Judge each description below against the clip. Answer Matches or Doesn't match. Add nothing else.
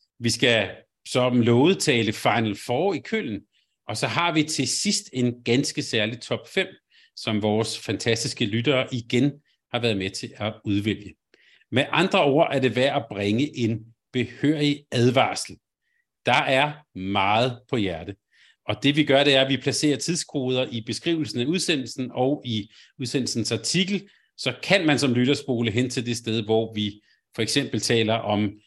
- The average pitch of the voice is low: Matches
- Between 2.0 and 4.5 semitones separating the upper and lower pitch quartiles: Matches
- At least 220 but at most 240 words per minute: Doesn't match